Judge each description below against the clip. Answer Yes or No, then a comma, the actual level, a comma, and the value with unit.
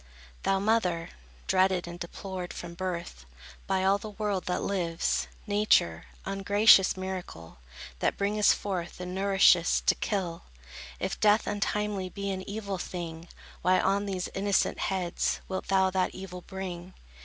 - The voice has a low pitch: No, high, 190 Hz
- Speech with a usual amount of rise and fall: No, narrow, 2.0 semitones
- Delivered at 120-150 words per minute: Yes, average, 140 wpm